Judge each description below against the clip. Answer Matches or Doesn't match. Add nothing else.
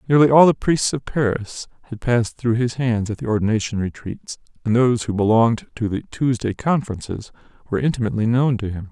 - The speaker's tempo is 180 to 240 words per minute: Matches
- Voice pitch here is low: Matches